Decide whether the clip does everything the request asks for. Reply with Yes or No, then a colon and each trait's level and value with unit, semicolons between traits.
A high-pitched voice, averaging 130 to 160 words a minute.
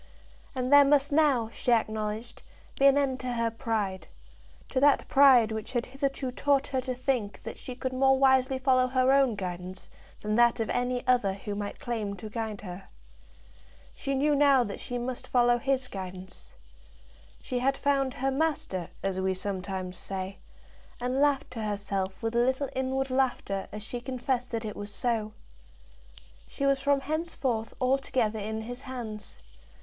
No: high, 245 Hz; average, 170 wpm